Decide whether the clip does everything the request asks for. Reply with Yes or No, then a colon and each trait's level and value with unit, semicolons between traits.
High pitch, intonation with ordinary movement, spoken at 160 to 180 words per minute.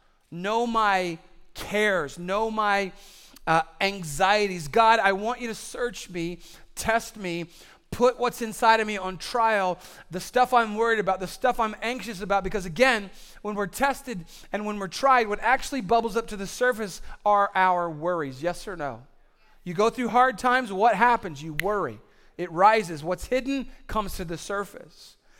Yes: high, 205 Hz; average, 4.2 semitones; average, 170 wpm